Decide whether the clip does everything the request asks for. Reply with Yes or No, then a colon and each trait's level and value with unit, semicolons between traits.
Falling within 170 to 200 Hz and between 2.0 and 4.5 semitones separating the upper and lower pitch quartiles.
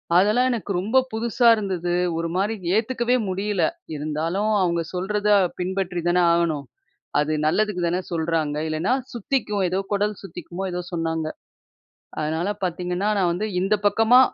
Yes: medium, 185 Hz; average, 3.8 semitones